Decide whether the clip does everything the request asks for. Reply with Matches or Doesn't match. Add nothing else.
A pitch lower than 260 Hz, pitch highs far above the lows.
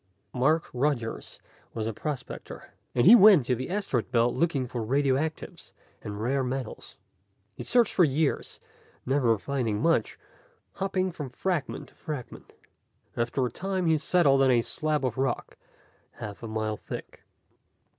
Doesn't match